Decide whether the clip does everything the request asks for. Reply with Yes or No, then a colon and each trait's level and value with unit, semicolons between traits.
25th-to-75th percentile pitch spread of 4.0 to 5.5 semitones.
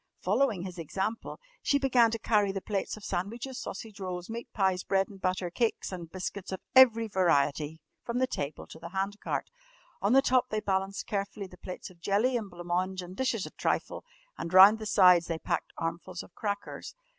No: average, 3.5 semitones